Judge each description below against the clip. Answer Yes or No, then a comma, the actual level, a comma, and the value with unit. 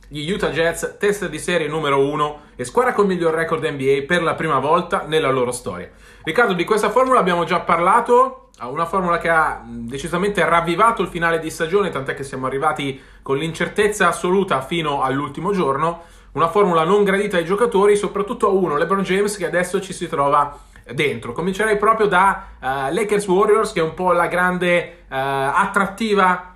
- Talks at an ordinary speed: No, fast, 180 wpm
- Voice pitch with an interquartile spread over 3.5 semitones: Yes, average, 4.0 semitones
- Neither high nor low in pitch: Yes, medium, 175 Hz